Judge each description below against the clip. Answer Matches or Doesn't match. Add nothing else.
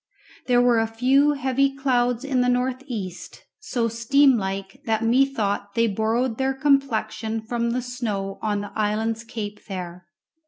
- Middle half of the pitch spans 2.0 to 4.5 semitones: Matches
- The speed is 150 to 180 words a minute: Matches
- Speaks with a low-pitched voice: Doesn't match